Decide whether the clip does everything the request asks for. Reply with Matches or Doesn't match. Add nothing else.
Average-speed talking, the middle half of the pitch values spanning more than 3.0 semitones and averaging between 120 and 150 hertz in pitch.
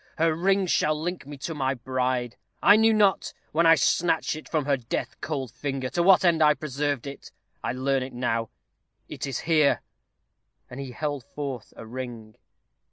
Matches